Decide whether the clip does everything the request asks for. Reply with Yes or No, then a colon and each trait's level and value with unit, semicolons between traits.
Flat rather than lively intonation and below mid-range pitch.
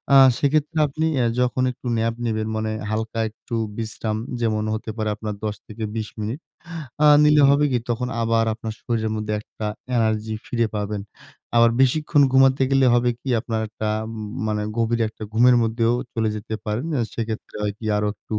Yes: narrow, 2.1 semitones; low, 115 Hz